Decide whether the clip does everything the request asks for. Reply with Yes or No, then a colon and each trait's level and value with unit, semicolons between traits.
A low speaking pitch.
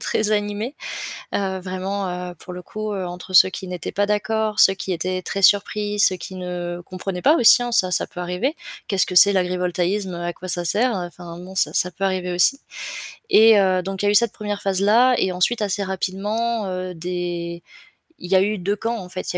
No: high, 190 Hz